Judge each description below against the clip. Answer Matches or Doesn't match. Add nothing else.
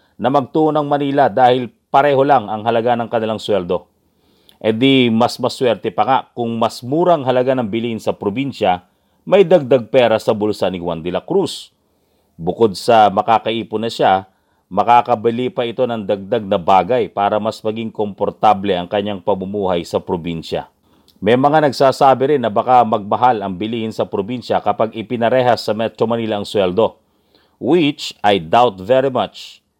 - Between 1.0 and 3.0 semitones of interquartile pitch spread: Doesn't match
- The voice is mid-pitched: Doesn't match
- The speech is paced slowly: Doesn't match